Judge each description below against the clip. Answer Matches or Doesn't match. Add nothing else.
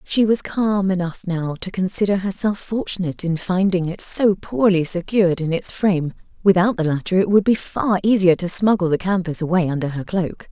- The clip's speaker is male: Doesn't match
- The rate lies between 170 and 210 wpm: Matches